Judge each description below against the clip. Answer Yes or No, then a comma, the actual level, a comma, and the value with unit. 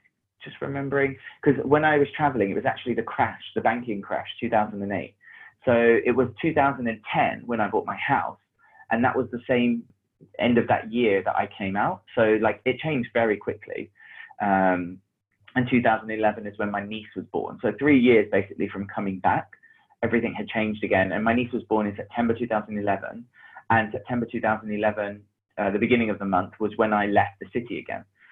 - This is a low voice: Yes, low, 110 Hz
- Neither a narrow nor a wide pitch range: Yes, average, 3.2 semitones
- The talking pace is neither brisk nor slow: Yes, average, 185 wpm